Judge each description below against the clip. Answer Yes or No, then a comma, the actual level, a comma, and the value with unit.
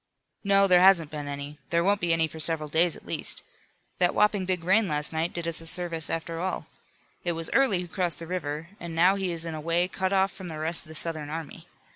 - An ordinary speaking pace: No, fast, 245 wpm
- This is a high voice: No, medium, 170 Hz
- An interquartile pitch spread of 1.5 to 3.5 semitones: Yes, narrow, 2.4 semitones